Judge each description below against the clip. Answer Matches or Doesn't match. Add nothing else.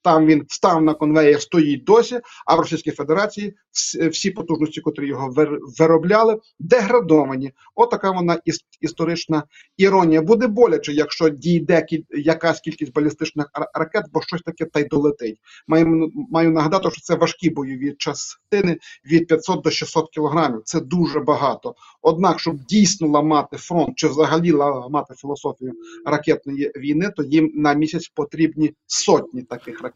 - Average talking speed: Matches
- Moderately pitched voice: Matches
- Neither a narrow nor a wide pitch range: Doesn't match